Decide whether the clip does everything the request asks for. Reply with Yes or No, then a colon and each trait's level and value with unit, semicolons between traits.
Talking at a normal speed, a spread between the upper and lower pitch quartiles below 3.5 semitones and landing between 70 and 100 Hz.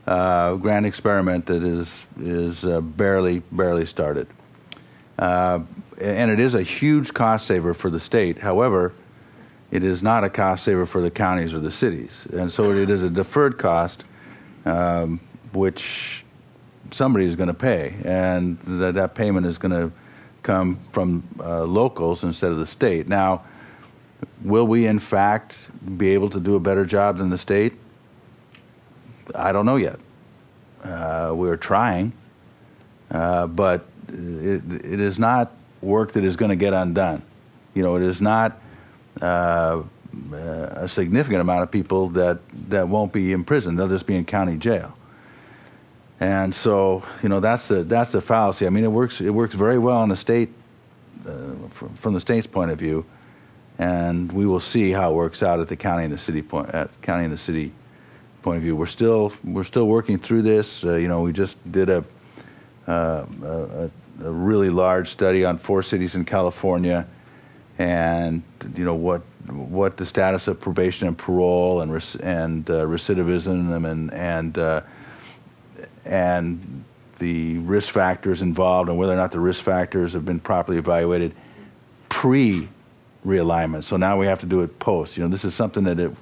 Yes: average, 175 wpm; average, 2.9 semitones; very low, 90 Hz